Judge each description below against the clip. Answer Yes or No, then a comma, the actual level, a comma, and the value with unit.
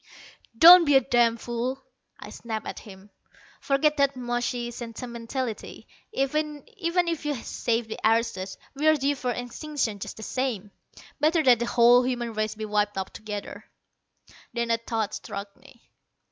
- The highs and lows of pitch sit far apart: No, average, 3.8 semitones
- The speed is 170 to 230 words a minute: No, average, 150 wpm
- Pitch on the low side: No, high, 240 Hz